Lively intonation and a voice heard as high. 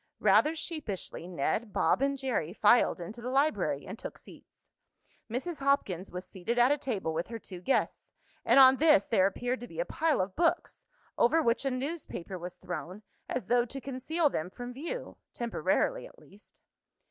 Yes: wide, 6.4 semitones; high, 245 Hz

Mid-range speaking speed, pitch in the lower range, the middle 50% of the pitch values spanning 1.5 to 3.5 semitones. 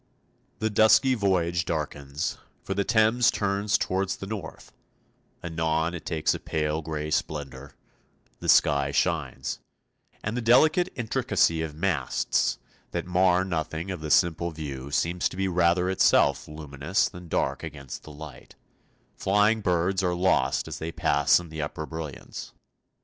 No: average, 145 wpm; very low, 85 Hz; average, 4.0 semitones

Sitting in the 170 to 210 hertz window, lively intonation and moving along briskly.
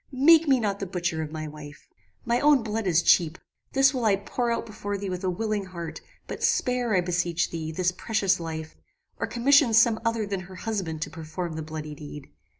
Yes: high, 190 Hz; wide, 5.7 semitones; fast, 210 wpm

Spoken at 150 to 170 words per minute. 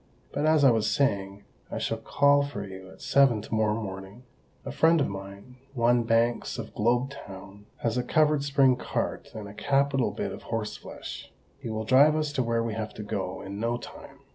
No: average, 195 wpm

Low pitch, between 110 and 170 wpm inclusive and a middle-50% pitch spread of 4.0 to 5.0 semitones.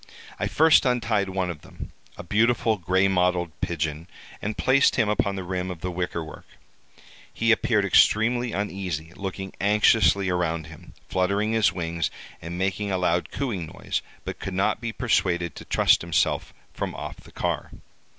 No: very low, 95 Hz; average, 165 wpm; average, 3.5 semitones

